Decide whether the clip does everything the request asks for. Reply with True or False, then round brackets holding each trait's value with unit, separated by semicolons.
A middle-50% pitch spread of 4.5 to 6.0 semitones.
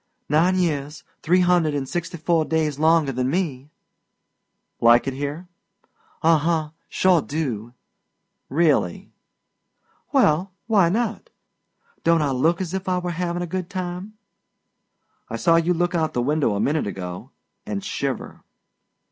False (3.9 semitones)